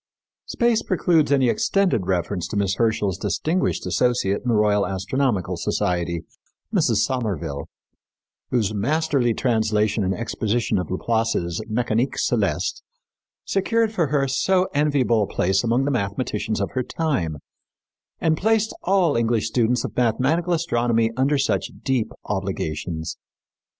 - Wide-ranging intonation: Yes, wide, 6.1 semitones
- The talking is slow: Yes, slow, 130 wpm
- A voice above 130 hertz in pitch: No, low, 115 Hz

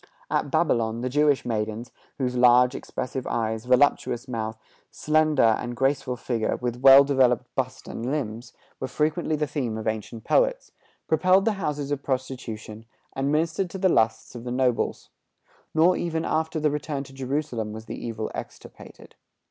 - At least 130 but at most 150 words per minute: No, average, 160 wpm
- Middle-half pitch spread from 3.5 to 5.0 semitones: Yes, average, 4.6 semitones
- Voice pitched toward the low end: Yes, low, 130 Hz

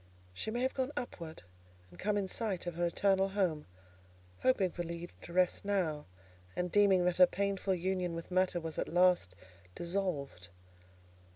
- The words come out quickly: No, average, 165 wpm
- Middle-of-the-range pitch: Yes, medium, 180 Hz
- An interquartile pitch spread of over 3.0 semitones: No, narrow, 2.6 semitones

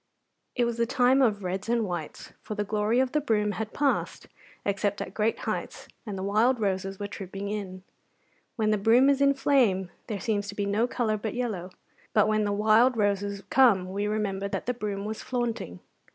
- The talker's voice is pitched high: Yes, high, 210 Hz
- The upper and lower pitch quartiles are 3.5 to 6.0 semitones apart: No, average, 2.9 semitones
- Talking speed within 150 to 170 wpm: No, average, 200 wpm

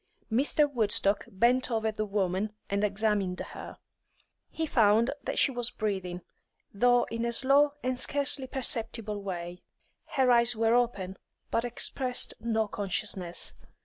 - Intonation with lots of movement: No, average, 3.6 semitones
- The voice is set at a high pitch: Yes, high, 225 Hz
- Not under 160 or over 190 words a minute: No, slow, 135 wpm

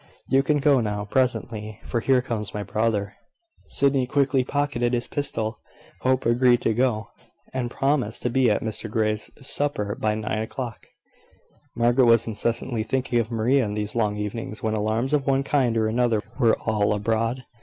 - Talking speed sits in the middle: Yes, average, 175 wpm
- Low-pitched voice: Yes, low, 115 Hz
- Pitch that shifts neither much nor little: Yes, average, 3.2 semitones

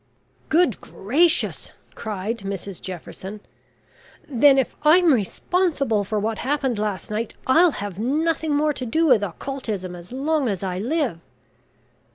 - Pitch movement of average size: No, wide, 6.7 semitones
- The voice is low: No, high, 240 Hz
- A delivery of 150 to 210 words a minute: No, slow, 135 wpm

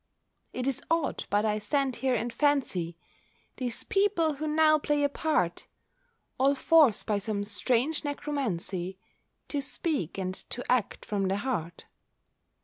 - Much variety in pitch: Yes, wide, 6.3 semitones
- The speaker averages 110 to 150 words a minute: Yes, average, 140 wpm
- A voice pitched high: Yes, very high, 255 Hz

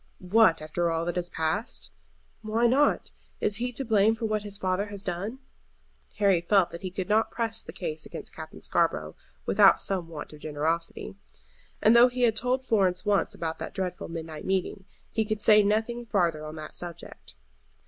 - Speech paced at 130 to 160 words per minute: No, average, 185 wpm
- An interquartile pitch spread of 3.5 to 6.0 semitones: Yes, average, 4.5 semitones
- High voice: Yes, high, 195 Hz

